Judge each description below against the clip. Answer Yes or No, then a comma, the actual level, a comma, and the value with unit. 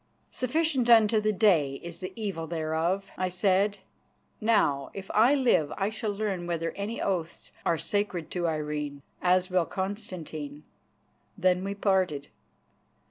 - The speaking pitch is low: No, medium, 185 Hz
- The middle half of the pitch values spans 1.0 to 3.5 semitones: No, average, 4.1 semitones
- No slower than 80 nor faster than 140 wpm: Yes, slow, 135 wpm